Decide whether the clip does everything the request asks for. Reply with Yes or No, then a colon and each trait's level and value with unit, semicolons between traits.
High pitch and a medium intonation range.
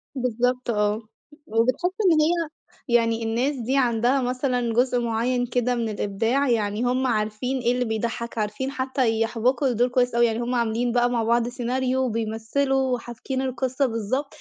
No: high, 245 Hz; narrow, 2.2 semitones